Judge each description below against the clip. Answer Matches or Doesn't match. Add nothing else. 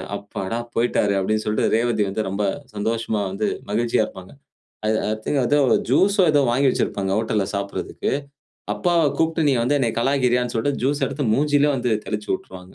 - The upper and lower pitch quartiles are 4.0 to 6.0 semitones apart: Matches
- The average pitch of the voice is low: Matches